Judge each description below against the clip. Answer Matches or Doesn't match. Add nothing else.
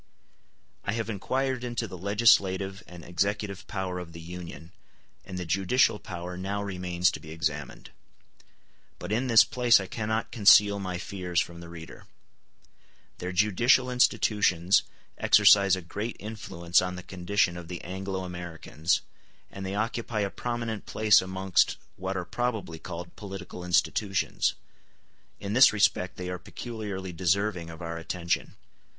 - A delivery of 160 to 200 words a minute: Doesn't match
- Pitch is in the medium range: Doesn't match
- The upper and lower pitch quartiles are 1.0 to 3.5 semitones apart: Matches